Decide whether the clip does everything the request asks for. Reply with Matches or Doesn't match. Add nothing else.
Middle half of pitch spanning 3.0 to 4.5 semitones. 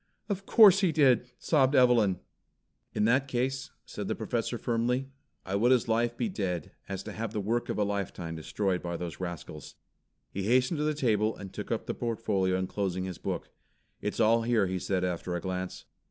Doesn't match